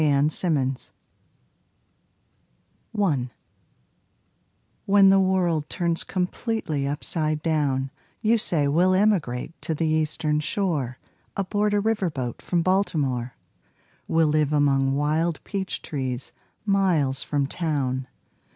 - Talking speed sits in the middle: No, slow, 105 wpm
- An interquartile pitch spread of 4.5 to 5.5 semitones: Yes, average, 5.0 semitones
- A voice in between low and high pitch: Yes, medium, 155 Hz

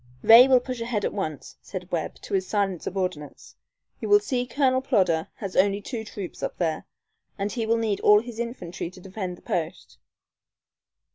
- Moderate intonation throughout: Yes, average, 4.5 semitones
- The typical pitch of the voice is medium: No, high, 200 Hz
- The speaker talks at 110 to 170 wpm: No, average, 180 wpm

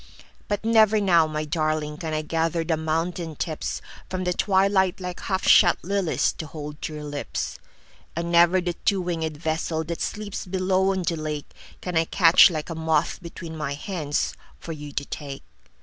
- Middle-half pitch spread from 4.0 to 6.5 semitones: No, average, 3.0 semitones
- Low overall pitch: No, medium, 165 Hz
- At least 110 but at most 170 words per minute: Yes, average, 155 wpm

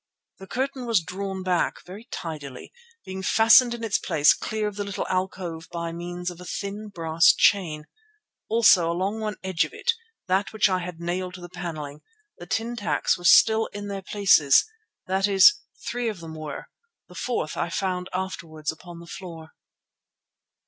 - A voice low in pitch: No, medium, 185 Hz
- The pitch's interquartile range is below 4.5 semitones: Yes, average, 3.3 semitones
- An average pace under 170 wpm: No, average, 175 wpm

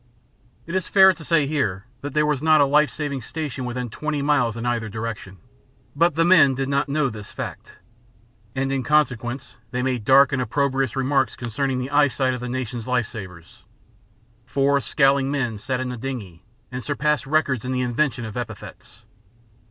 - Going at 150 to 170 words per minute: No, average, 185 wpm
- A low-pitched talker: Yes, low, 130 Hz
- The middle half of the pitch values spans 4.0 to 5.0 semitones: No, average, 2.9 semitones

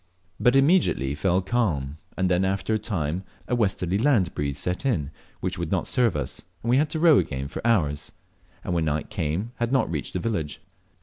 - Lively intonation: Yes, wide, 7.8 semitones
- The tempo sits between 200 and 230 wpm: Yes, fast, 205 wpm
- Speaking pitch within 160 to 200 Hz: No, very low, 95 Hz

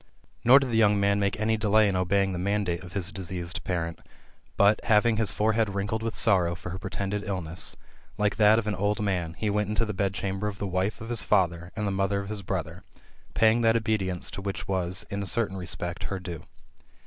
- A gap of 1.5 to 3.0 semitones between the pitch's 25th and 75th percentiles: Yes, narrow, 2.4 semitones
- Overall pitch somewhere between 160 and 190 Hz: No, low, 100 Hz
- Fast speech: Yes, fast, 225 wpm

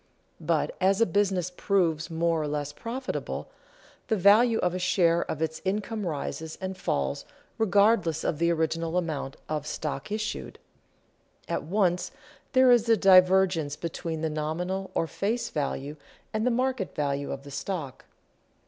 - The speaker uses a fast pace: No, average, 150 wpm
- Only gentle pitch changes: No, average, 4.3 semitones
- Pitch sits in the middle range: Yes, medium, 180 Hz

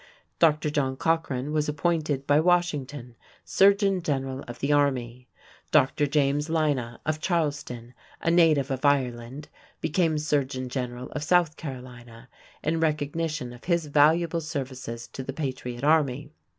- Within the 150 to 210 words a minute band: No, slow, 135 wpm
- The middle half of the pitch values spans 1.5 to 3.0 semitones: No, average, 3.5 semitones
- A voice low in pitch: No, medium, 145 Hz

